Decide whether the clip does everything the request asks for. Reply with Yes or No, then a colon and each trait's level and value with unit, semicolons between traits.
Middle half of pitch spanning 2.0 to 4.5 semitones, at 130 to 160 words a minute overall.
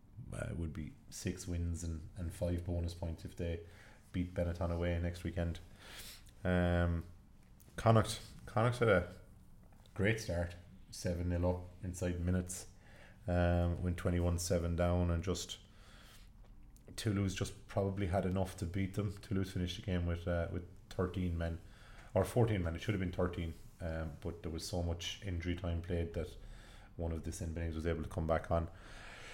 No: average, 2.8 semitones; average, 170 wpm